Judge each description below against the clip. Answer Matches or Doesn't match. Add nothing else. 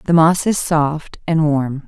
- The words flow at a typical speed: Matches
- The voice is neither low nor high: Matches